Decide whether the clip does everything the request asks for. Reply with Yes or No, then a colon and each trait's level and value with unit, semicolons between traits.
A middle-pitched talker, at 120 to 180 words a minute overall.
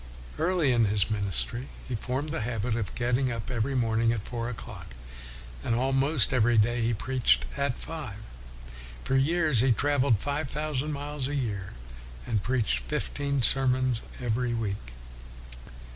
No: low, 125 Hz; average, 150 wpm